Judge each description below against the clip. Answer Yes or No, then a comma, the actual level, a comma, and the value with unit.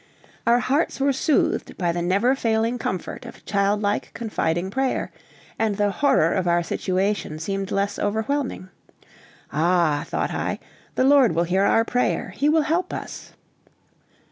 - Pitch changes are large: Yes, wide, 5.7 semitones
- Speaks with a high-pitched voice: Yes, high, 205 Hz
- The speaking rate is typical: Yes, average, 150 wpm